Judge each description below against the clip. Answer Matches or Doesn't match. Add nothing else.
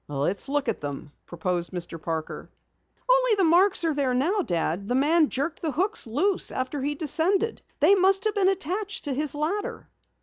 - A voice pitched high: Matches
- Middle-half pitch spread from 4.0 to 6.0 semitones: Doesn't match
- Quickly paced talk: Doesn't match